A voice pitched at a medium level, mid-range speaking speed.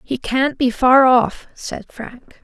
No: very high, 250 Hz; average, 170 wpm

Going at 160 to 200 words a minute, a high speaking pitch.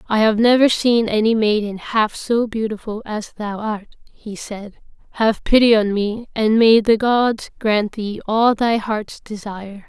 Yes: average, 170 wpm; high, 220 Hz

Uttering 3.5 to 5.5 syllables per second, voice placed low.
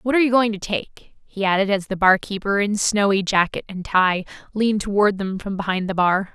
No: 5.4 syllables/s; high, 200 Hz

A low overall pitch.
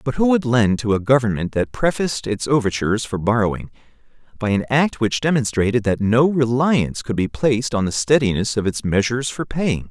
Yes: low, 120 Hz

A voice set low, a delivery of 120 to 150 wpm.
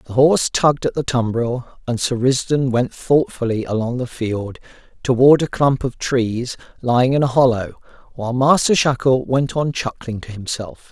No: low, 125 Hz; average, 170 wpm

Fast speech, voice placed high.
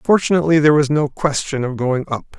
No: fast, 225 wpm; medium, 145 Hz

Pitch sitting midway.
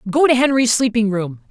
No: high, 230 Hz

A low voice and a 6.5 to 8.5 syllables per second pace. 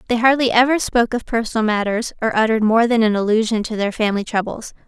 No: high, 225 Hz; 6.7 syllables/s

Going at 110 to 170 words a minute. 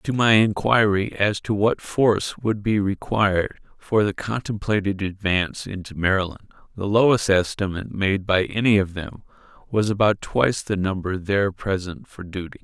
Yes: average, 155 wpm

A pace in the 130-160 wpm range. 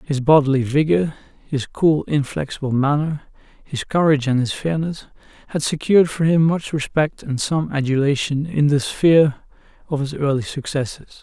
Yes: average, 150 wpm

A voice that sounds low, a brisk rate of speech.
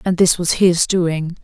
No: medium, 175 Hz; fast, 210 wpm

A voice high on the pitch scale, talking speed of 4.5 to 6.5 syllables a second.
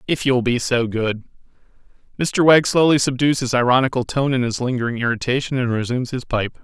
No: low, 125 Hz; 5.8 syllables/s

